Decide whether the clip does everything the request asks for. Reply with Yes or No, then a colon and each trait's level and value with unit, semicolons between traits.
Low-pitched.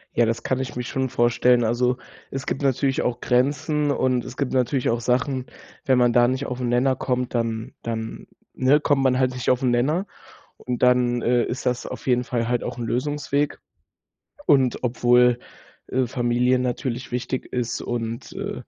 Yes: low, 125 Hz